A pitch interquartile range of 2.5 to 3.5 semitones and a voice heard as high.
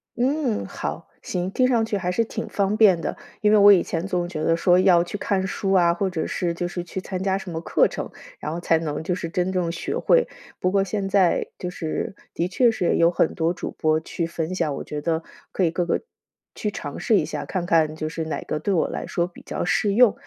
No: average, 2.9 semitones; medium, 180 Hz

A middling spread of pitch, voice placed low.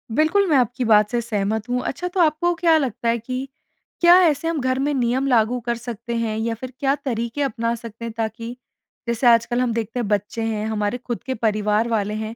No: average, 3.1 semitones; high, 235 Hz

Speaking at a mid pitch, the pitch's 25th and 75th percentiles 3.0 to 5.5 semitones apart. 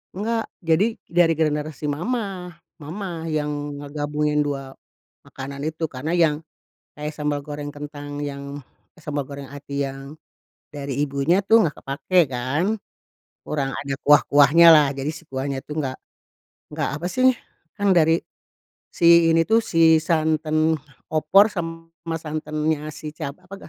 No: medium, 150 Hz; narrow, 2.5 semitones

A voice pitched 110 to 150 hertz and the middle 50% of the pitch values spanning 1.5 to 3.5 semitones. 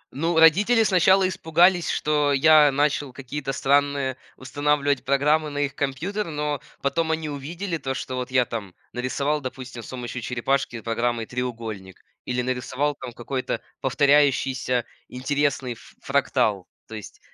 Yes: medium, 140 Hz; average, 3.0 semitones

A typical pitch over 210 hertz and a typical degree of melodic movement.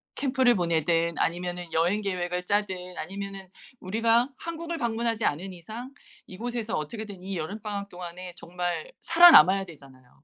No: high, 190 Hz; average, 4.4 semitones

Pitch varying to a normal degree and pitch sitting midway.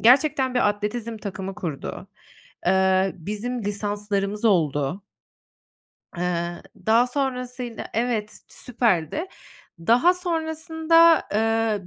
No: average, 4.6 semitones; high, 220 Hz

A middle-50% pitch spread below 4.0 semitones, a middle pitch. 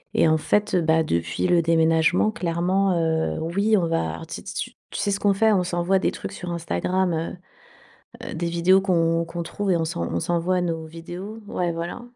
Yes: narrow, 2.4 semitones; medium, 170 Hz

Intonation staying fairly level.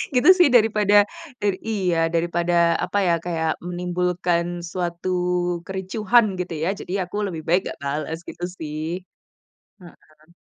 Yes: narrow, 2.3 semitones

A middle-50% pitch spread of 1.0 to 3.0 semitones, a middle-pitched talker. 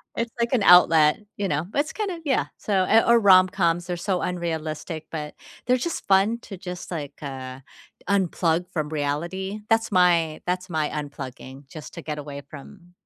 No: average, 4.5 semitones; medium, 175 Hz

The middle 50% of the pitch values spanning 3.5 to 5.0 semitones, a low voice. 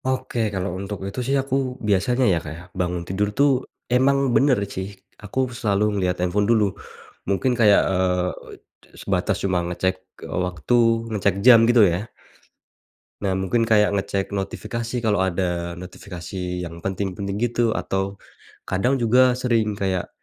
Yes: average, 4.2 semitones; low, 100 Hz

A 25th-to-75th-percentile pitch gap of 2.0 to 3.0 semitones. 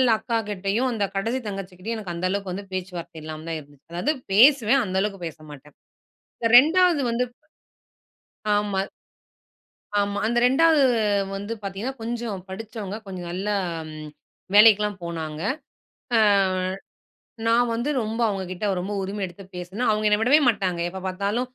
No: average, 3.8 semitones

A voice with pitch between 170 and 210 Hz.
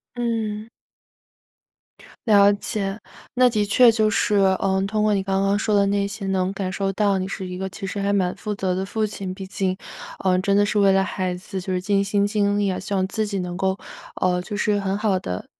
Yes: high, 200 Hz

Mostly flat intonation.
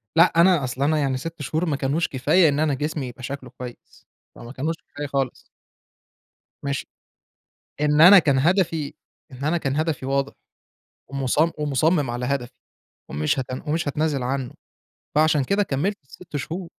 No: average, 3.2 semitones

